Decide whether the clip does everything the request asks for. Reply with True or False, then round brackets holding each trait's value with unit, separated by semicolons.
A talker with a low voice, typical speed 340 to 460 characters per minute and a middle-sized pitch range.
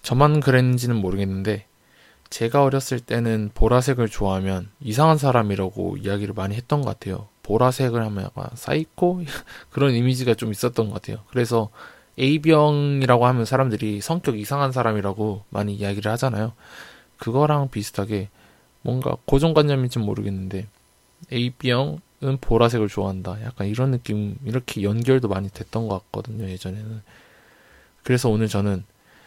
True (115 Hz; 355 characters per minute; 4.4 semitones)